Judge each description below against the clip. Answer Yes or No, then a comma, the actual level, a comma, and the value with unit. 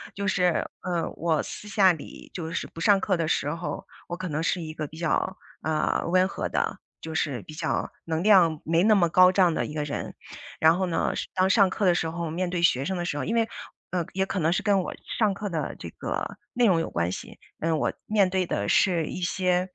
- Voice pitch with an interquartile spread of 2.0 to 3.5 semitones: Yes, average, 2.9 semitones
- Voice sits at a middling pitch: Yes, medium, 175 Hz